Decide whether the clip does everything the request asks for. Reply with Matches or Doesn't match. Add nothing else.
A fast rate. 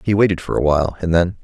Matches